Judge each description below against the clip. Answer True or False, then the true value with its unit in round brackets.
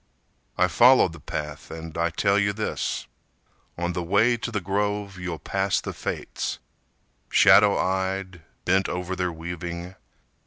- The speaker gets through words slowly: False (145 wpm)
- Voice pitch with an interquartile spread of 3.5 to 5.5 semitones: False (2.7 semitones)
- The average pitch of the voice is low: True (95 Hz)